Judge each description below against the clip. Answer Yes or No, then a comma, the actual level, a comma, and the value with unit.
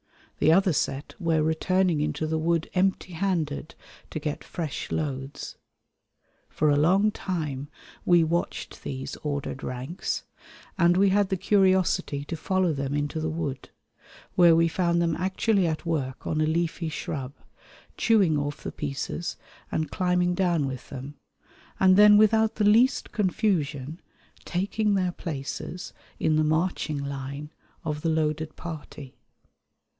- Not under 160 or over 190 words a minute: No, average, 140 wpm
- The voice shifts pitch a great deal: No, average, 3.9 semitones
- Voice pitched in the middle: Yes, medium, 160 Hz